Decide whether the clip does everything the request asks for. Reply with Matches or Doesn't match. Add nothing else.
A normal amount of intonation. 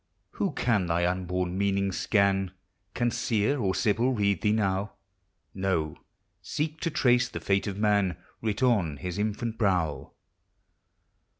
Matches